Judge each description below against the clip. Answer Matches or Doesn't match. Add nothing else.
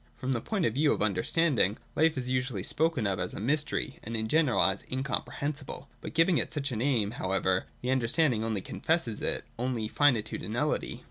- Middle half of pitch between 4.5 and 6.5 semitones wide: Matches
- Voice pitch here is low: Matches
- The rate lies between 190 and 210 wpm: Matches